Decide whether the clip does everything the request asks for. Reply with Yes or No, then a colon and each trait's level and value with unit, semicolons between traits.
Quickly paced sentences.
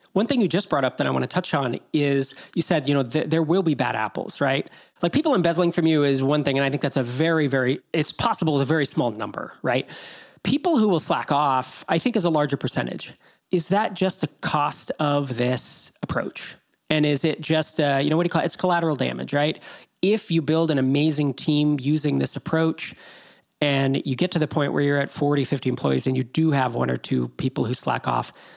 Yes: fast, 235 wpm